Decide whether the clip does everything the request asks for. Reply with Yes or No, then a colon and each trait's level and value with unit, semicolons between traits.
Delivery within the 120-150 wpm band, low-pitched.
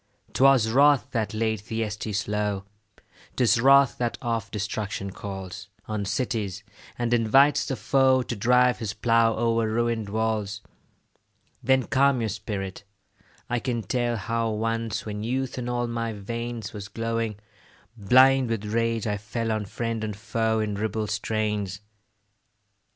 Yes: average, 140 wpm; low, 115 Hz